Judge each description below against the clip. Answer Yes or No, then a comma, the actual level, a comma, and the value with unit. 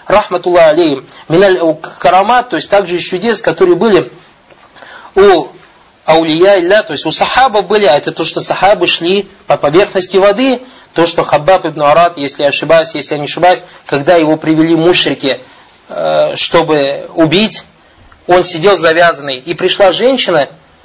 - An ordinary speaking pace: Yes, average, 145 wpm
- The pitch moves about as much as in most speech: Yes, average, 4.0 semitones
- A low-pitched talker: No, medium, 175 Hz